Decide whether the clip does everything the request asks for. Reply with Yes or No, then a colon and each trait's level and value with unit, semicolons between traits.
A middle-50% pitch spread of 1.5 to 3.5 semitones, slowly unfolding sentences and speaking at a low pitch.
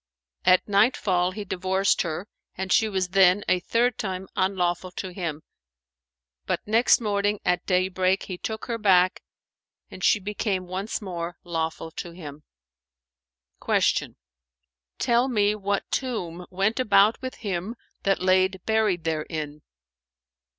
No: average, 2.8 semitones; slow, 130 wpm; high, 190 Hz